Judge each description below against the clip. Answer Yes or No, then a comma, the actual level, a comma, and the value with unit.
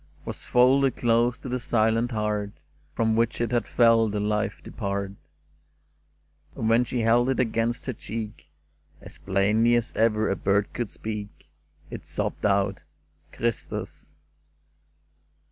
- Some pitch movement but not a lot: No, narrow, 2.2 semitones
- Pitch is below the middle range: Yes, low, 115 Hz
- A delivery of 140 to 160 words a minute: Yes, average, 145 wpm